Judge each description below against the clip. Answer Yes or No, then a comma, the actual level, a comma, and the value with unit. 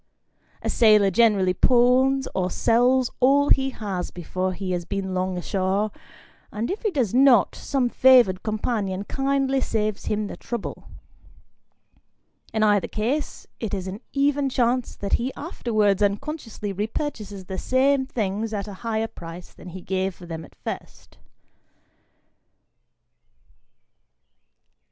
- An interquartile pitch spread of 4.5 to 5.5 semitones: Yes, average, 5.1 semitones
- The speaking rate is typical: No, slow, 130 wpm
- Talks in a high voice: Yes, high, 215 Hz